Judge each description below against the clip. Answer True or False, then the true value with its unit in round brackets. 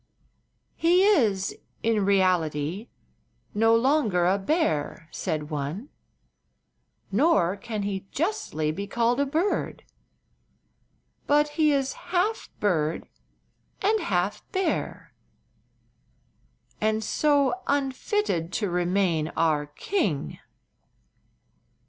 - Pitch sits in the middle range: False (210 Hz)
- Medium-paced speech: False (90 wpm)